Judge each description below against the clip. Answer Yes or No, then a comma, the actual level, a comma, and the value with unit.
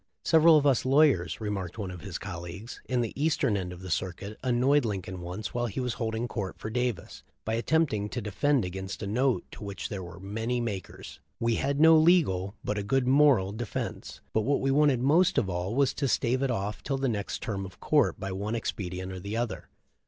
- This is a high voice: No, low, 110 Hz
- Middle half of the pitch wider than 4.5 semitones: Yes, wide, 5.5 semitones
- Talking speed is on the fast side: Yes, fast, 215 wpm